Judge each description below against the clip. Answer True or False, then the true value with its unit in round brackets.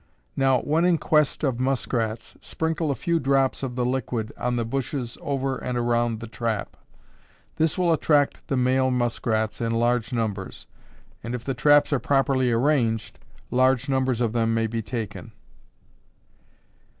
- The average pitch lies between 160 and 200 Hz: False (125 Hz)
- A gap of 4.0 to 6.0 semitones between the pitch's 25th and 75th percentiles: False (2.9 semitones)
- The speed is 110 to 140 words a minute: False (155 wpm)